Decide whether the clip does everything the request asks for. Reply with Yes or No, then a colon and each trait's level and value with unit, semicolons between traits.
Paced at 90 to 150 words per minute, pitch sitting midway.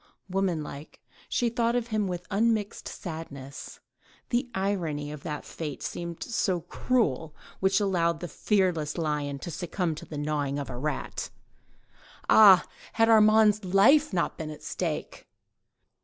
Yes: average, 140 wpm; medium, 175 Hz